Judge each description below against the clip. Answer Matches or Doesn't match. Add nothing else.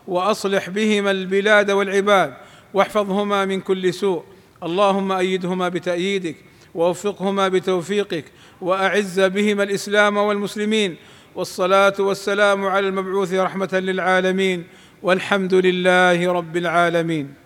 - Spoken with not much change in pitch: Matches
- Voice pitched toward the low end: Doesn't match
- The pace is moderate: Matches